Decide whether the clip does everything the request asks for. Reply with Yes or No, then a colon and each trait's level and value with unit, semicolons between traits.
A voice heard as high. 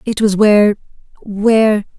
Yes: high, 210 Hz